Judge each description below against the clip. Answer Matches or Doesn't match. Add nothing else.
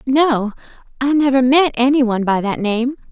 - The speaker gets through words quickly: Doesn't match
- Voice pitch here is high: Matches